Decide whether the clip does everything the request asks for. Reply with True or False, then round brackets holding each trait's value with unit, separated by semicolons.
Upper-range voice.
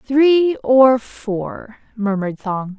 True (235 Hz)